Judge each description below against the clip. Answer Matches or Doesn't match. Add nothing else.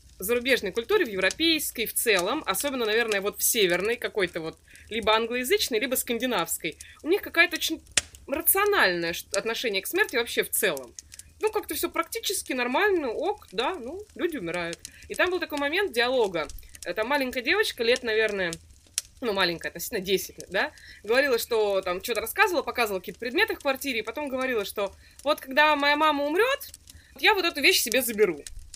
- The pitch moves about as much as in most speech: Doesn't match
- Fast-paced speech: Matches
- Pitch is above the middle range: Matches